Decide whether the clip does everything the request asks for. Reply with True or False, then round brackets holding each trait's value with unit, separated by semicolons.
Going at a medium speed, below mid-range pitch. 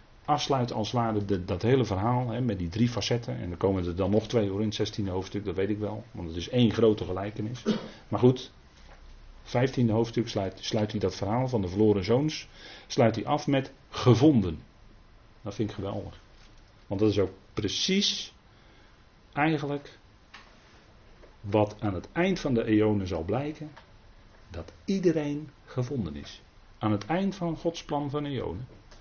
True (170 wpm; 110 Hz)